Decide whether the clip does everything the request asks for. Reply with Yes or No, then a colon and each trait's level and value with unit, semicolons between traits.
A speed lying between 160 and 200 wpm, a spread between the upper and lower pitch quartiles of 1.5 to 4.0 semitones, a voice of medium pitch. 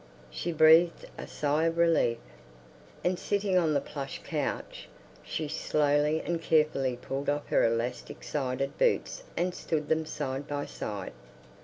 No: average, 145 wpm; average, 3.2 semitones; medium, 150 Hz